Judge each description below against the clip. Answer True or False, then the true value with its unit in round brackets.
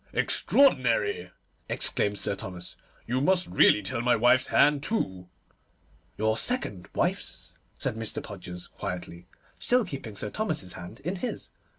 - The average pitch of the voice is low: True (110 Hz)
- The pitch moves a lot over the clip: True (7.7 semitones)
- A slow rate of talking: True (130 wpm)